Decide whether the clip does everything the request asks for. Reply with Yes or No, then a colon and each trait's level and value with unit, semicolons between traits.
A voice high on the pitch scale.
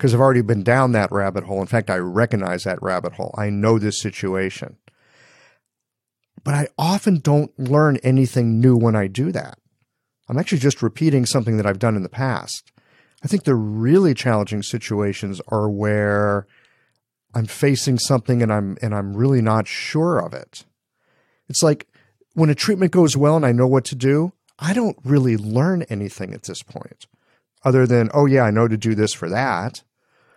No: low, 120 Hz